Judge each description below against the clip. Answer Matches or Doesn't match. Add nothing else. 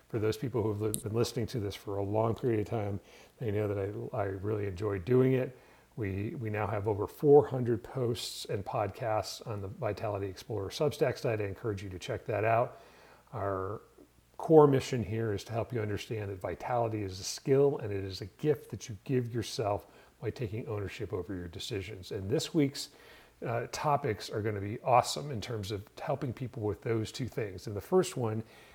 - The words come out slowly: Doesn't match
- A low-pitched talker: Matches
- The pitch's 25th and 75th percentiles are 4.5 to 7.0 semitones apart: Doesn't match